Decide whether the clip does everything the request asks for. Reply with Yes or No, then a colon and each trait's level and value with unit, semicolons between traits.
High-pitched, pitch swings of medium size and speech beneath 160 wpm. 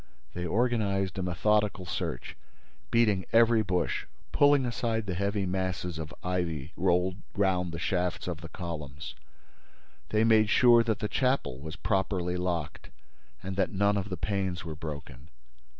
No: very low, 95 Hz; average, 3.5 semitones; average, 150 wpm